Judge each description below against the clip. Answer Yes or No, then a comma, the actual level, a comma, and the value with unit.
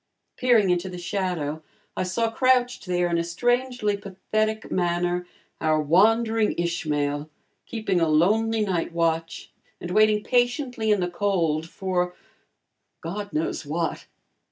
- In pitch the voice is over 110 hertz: Yes, medium, 185 Hz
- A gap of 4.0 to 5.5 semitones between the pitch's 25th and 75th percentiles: Yes, average, 4.4 semitones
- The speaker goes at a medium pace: No, slow, 130 wpm